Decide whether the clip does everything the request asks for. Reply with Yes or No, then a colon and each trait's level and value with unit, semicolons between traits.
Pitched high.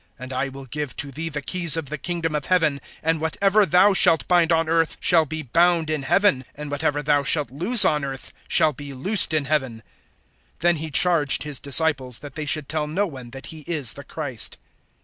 No: medium, 150 Hz